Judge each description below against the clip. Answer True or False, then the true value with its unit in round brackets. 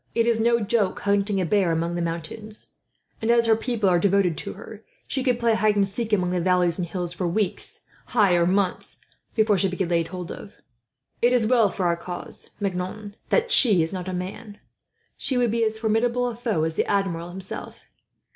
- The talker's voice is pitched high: True (200 Hz)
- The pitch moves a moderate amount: True (3.9 semitones)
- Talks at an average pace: False (210 wpm)